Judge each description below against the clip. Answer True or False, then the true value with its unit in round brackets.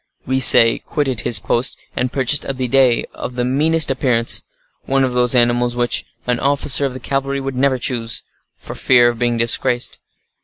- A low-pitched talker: True (125 Hz)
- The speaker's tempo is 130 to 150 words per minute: False (175 wpm)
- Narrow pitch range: True (2.0 semitones)